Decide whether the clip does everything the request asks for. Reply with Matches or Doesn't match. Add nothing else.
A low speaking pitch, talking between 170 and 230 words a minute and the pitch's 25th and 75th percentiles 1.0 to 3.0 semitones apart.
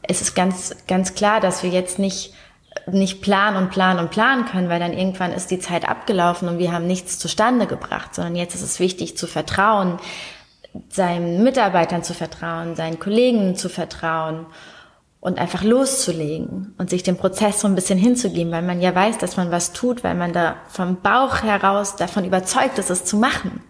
Doesn't match